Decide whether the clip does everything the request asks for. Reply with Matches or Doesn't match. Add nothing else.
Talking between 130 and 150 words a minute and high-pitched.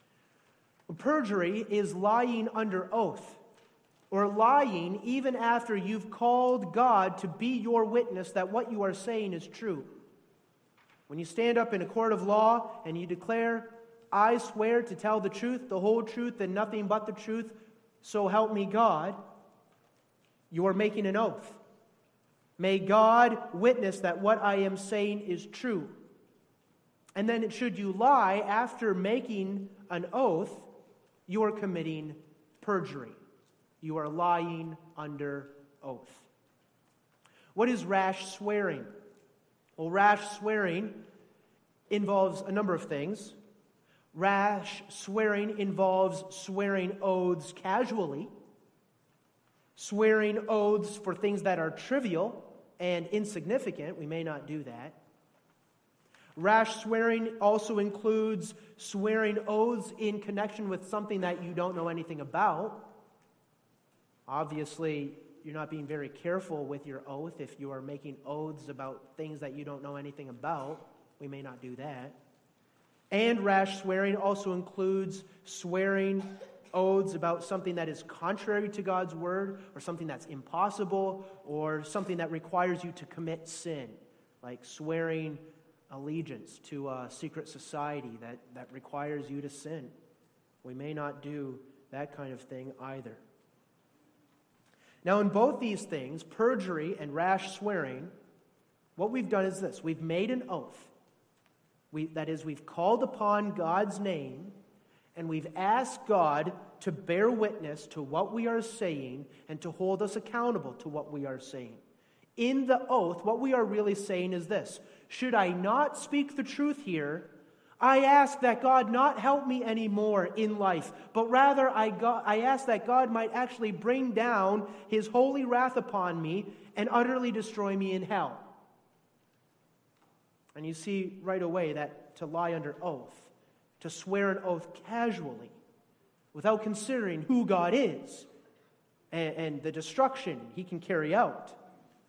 Matches